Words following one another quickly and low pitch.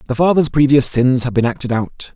Yes: fast, 225 wpm; low, 130 Hz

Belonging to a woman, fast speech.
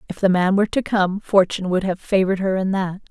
Yes: female; fast, 250 wpm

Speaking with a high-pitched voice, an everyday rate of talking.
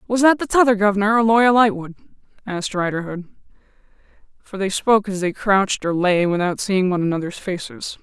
Yes: high, 200 Hz; average, 170 wpm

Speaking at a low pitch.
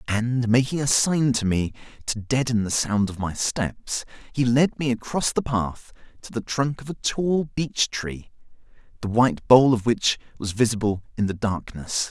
Yes: low, 120 Hz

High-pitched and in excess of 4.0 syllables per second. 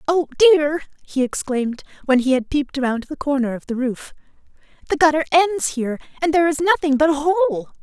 Yes: very high, 295 Hz; 5.7 syllables/s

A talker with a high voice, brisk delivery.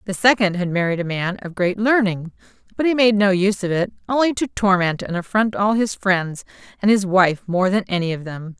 Yes: high, 195 Hz; fast, 225 wpm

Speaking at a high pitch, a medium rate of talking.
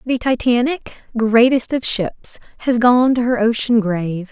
Yes: high, 235 Hz; average, 155 wpm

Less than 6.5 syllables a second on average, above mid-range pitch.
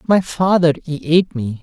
No: 5.2 syllables/s; medium, 160 Hz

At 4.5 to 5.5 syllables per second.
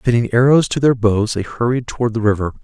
No: 6.0 syllables/s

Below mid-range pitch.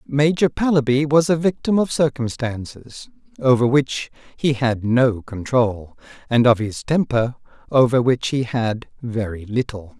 Yes: low, 130 Hz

